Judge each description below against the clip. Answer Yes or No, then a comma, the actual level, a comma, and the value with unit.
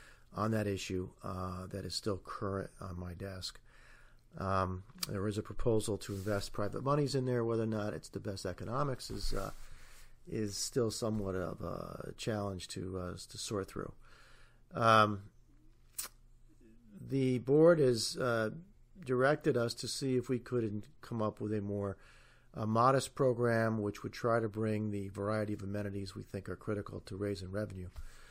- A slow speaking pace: No, average, 165 wpm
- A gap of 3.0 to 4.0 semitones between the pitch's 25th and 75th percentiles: Yes, average, 3.5 semitones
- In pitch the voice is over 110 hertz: No, low, 105 Hz